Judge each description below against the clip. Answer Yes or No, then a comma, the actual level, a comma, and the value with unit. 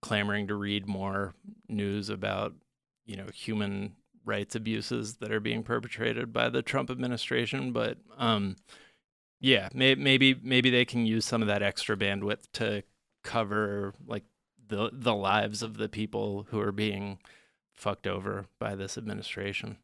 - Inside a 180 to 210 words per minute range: No, average, 150 wpm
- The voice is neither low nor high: No, low, 105 Hz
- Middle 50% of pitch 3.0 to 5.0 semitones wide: No, narrow, 2.5 semitones